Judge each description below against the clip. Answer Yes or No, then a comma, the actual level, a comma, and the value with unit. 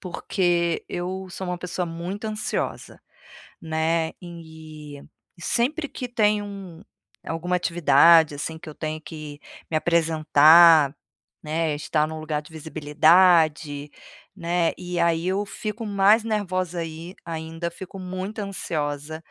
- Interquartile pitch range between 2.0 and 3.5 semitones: Yes, average, 2.8 semitones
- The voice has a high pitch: No, medium, 170 Hz